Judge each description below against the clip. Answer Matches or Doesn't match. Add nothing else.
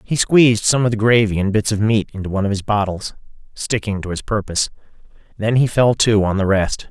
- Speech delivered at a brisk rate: Matches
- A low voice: Matches